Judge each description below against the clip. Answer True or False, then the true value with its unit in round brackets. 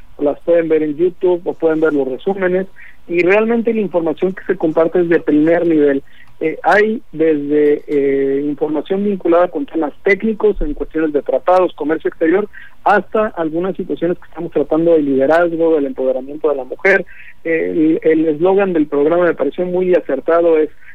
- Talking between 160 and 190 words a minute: True (170 wpm)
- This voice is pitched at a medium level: True (165 Hz)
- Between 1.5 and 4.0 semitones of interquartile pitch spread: True (3.3 semitones)